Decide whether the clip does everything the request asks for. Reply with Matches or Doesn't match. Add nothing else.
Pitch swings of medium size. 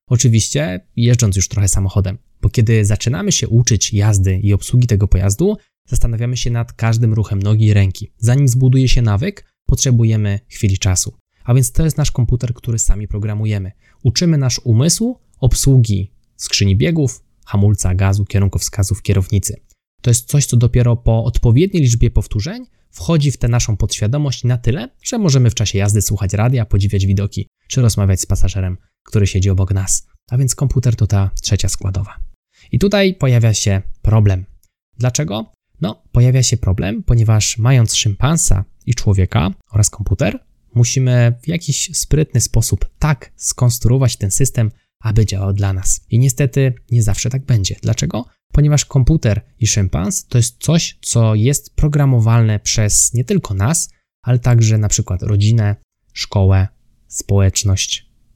Matches